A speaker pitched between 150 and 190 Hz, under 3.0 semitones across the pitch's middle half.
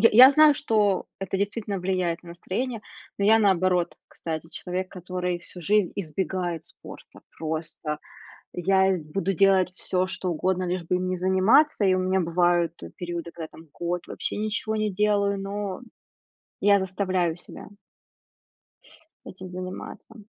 Yes: medium, 185 Hz; narrow, 2.4 semitones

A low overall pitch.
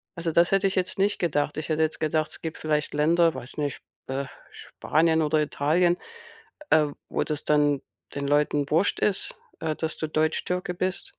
No: medium, 155 Hz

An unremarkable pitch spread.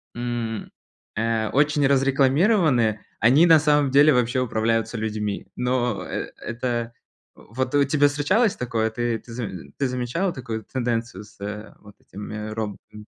Yes: average, 3.7 semitones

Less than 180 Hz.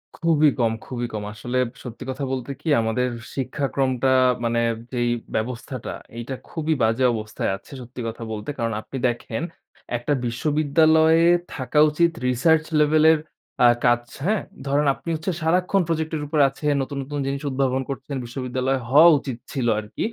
Yes: low, 135 Hz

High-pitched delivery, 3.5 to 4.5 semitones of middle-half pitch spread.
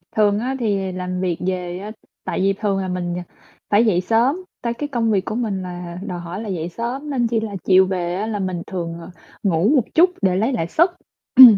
Yes: high, 195 Hz; average, 4.0 semitones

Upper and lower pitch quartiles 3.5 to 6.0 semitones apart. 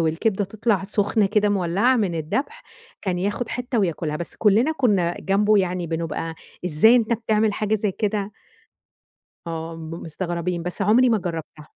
Yes: average, 4.3 semitones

